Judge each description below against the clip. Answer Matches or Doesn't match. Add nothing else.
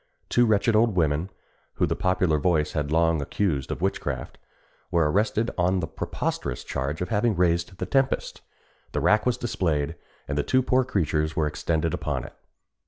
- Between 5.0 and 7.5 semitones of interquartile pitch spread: Matches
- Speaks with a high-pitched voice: Doesn't match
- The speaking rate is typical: Matches